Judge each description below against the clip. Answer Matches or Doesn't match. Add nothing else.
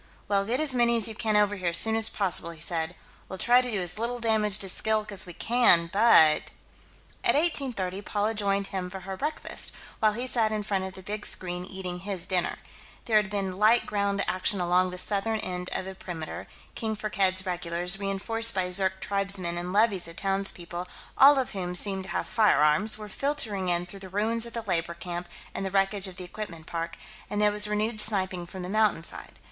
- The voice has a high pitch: Matches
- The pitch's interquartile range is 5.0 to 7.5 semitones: Doesn't match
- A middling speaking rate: Doesn't match